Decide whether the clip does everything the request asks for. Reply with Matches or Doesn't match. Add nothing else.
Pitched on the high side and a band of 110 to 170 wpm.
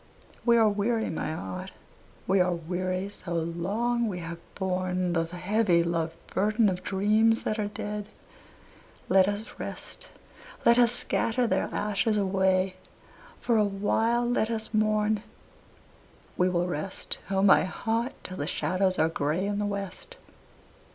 Matches